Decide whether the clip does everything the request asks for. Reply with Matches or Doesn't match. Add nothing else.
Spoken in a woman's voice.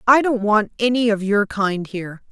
Matches